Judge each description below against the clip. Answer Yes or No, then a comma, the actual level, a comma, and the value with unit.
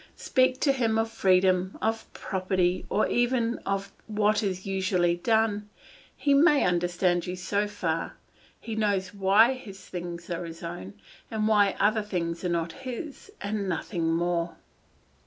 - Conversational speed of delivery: Yes, average, 150 wpm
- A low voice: No, high, 195 Hz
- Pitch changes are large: No, average, 3.8 semitones